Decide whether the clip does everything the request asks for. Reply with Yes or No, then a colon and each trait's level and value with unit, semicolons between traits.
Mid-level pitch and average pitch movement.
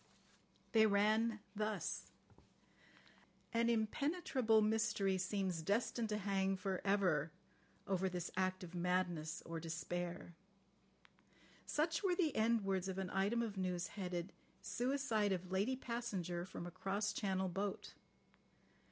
No: high, 195 Hz; average, 3.2 semitones